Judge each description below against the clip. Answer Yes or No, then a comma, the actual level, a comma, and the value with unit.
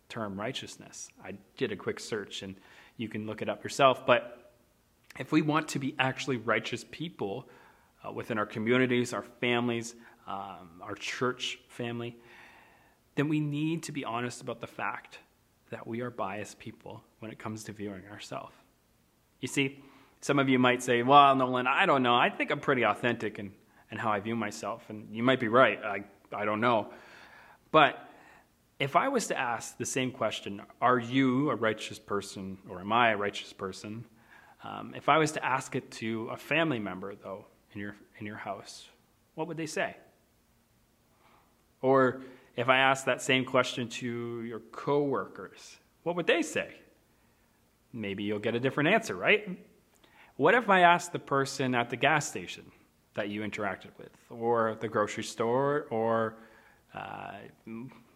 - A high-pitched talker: No, low, 120 Hz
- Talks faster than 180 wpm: No, average, 170 wpm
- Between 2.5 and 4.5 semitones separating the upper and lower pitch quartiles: Yes, average, 3.4 semitones